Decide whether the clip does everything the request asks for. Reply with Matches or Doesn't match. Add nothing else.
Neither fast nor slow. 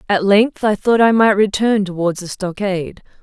Matches